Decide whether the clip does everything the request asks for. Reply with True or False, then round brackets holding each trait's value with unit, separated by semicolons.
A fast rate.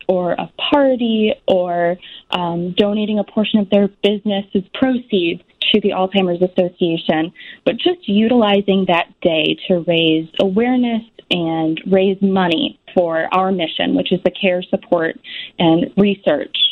False (135 wpm)